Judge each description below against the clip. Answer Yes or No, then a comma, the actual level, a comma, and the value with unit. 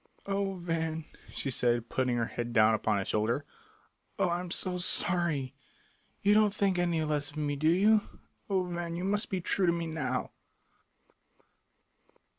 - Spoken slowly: No, average, 165 wpm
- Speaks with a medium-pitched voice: Yes, medium, 165 Hz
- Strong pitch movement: Yes, wide, 5.8 semitones